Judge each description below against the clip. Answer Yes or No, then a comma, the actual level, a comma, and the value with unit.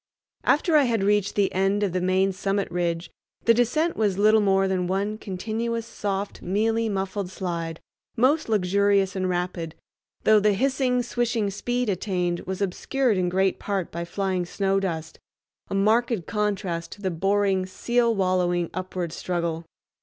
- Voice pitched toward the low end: No, high, 195 Hz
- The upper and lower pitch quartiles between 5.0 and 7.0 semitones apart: No, average, 2.9 semitones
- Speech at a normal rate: Yes, average, 155 wpm